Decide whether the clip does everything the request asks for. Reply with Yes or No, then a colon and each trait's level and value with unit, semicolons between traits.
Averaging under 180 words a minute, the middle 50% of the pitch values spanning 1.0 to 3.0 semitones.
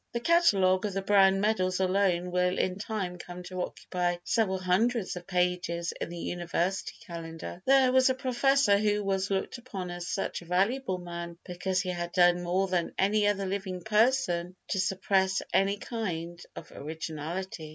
Yes: average, 170 wpm; narrow, 2.6 semitones